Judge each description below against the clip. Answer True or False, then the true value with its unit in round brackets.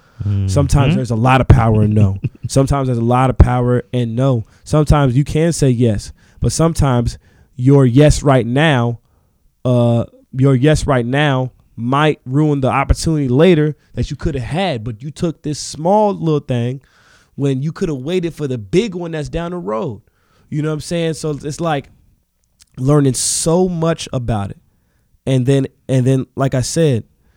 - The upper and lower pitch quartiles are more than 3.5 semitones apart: True (4.1 semitones)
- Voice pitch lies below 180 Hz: True (135 Hz)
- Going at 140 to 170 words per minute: False (180 wpm)